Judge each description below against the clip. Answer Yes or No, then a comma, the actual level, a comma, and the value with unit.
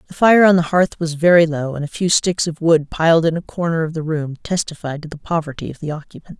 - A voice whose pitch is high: No, medium, 165 Hz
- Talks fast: Yes, fast, 265 wpm